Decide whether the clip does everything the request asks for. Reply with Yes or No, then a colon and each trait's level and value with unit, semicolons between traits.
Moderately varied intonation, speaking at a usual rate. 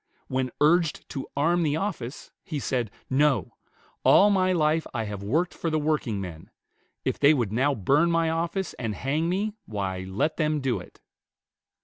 No: wide, 5.7 semitones; average, 165 wpm